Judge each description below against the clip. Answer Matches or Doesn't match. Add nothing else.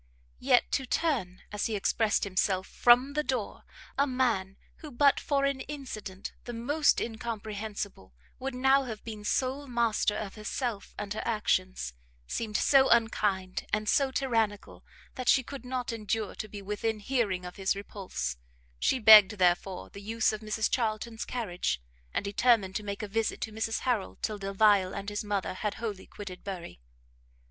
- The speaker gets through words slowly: Doesn't match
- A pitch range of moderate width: Matches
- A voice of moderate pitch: Doesn't match